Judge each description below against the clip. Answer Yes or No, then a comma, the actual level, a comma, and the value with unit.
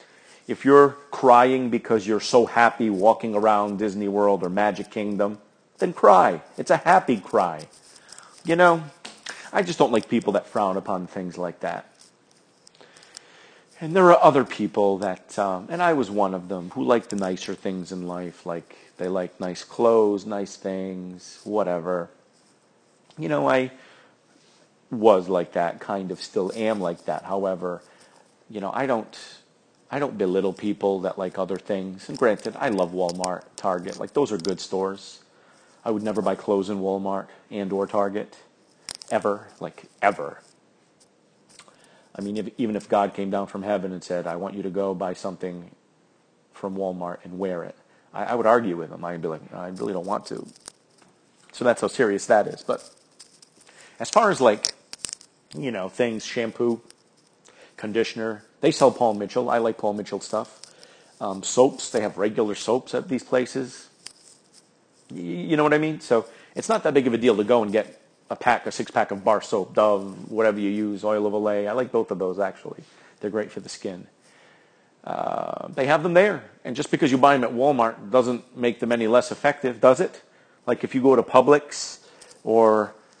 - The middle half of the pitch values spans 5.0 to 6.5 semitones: No, average, 3.9 semitones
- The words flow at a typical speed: Yes, average, 185 wpm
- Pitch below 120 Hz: Yes, low, 105 Hz